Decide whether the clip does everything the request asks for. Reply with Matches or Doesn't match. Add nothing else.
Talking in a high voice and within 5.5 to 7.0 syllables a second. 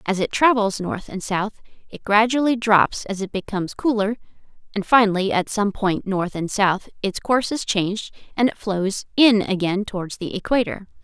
Doesn't match